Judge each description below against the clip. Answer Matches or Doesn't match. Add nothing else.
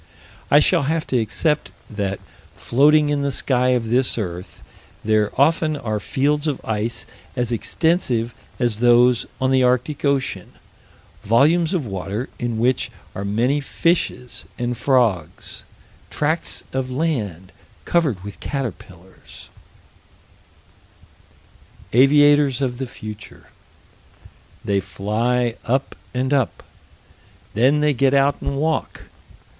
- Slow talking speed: Matches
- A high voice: Doesn't match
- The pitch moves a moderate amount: Matches